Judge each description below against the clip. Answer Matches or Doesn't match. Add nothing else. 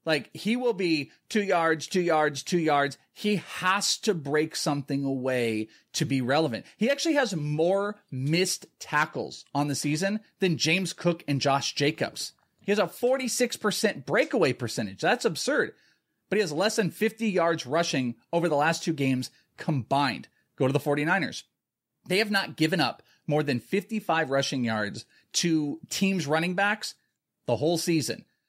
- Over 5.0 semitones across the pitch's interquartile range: Matches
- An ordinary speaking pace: Matches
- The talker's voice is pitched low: Doesn't match